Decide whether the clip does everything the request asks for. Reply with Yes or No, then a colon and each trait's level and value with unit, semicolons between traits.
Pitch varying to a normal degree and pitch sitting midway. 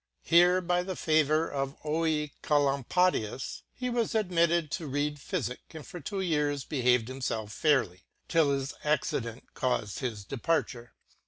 Yes: average, 4.5 semitones; medium, 150 Hz